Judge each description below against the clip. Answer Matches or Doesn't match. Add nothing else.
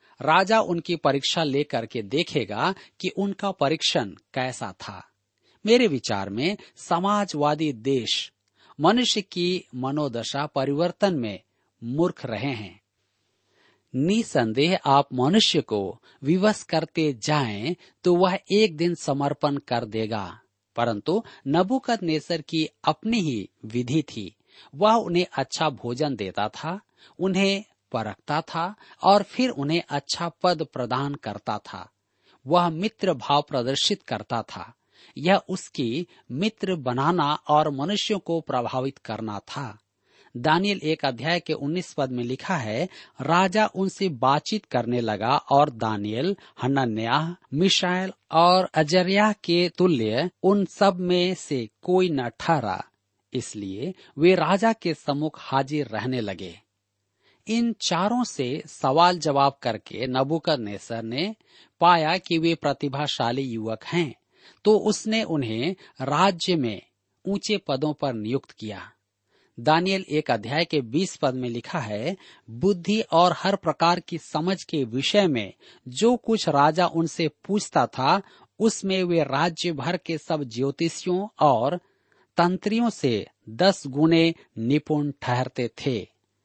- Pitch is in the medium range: Matches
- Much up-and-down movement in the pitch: Matches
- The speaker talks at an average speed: Matches